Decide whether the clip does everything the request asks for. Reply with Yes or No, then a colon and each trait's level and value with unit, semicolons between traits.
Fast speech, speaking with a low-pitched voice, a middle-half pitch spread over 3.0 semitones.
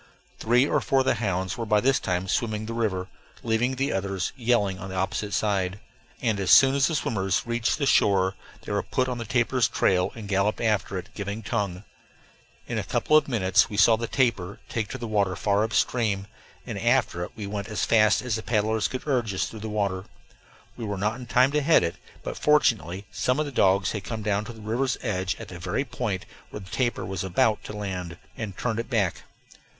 Yes: fast, 225 wpm; low, 105 Hz; average, 3.6 semitones